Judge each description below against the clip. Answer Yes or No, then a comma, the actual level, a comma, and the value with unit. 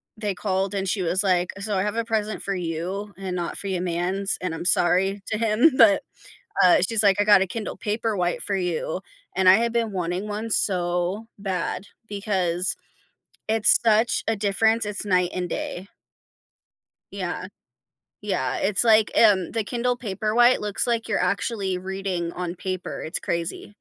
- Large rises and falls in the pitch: No, average, 3.0 semitones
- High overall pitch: Yes, high, 195 Hz